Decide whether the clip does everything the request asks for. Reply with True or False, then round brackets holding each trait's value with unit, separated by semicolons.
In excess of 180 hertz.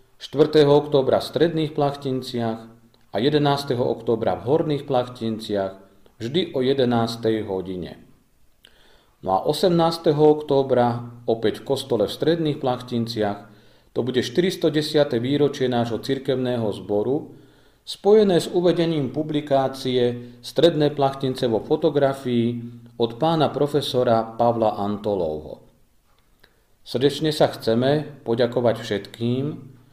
False (130 Hz)